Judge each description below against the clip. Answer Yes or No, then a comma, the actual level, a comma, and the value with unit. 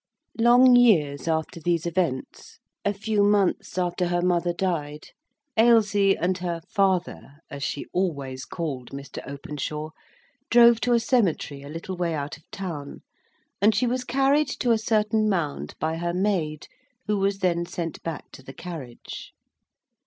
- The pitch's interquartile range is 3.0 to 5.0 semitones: No, wide, 5.4 semitones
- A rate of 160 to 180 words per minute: No, average, 150 wpm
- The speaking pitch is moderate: Yes, medium, 175 Hz